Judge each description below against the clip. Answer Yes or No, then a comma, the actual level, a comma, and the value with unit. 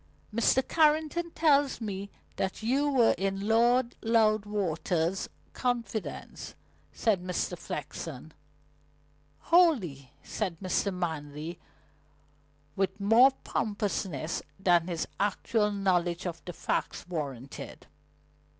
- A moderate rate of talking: No, slow, 95 wpm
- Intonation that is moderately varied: Yes, average, 5.0 semitones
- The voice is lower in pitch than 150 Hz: No, high, 200 Hz